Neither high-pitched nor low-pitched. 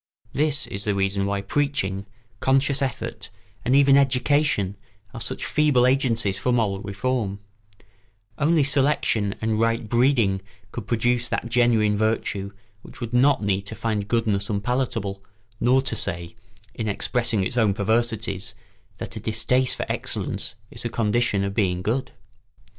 No: low, 115 Hz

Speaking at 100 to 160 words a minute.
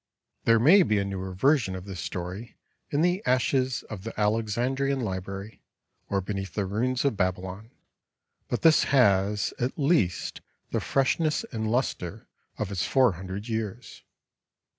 Yes: average, 150 wpm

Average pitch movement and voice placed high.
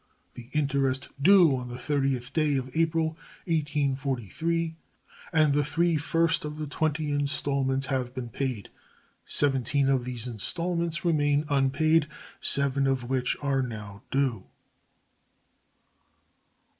No: average, 3.1 semitones; medium, 140 Hz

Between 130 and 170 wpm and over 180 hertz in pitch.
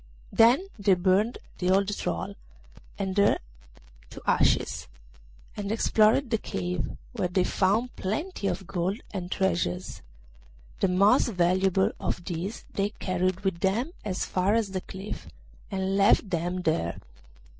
Yes: slow, 135 wpm; high, 190 Hz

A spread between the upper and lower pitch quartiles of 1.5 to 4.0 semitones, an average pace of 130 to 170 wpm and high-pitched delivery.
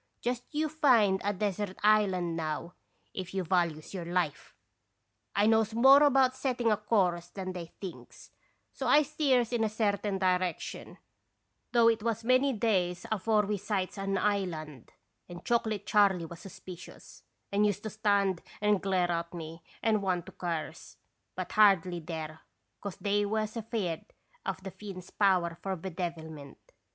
Yes: average, 3.6 semitones; average, 160 wpm; high, 195 Hz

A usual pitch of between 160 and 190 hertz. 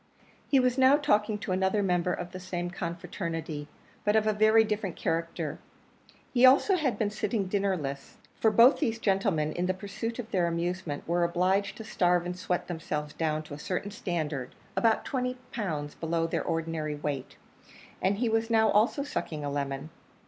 Yes: medium, 185 Hz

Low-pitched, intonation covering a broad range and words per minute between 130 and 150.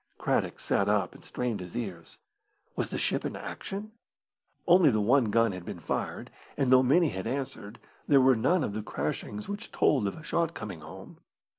No: low, 120 Hz; wide, 6.1 semitones; average, 190 wpm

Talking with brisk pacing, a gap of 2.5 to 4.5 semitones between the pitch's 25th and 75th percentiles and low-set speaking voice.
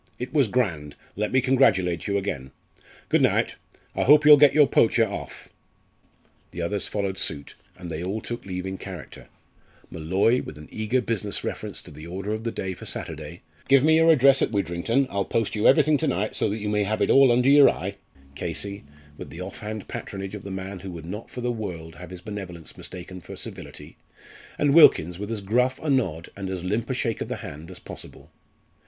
No: fast, 210 wpm; average, 5.1 semitones; low, 100 Hz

